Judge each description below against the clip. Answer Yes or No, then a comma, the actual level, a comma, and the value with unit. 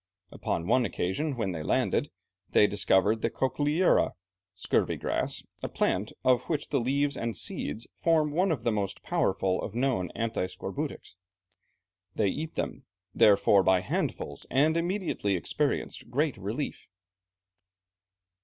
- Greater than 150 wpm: No, slow, 135 wpm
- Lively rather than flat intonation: Yes, wide, 7.1 semitones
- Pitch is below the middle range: Yes, low, 115 Hz